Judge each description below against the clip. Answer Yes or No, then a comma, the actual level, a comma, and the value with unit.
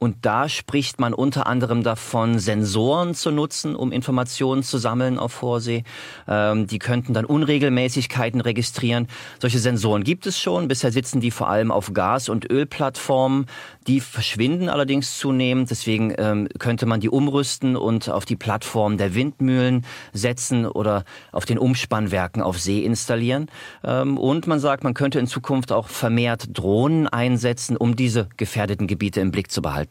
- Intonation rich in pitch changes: No, average, 3.1 semitones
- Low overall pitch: Yes, low, 120 Hz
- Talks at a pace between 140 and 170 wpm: Yes, average, 160 wpm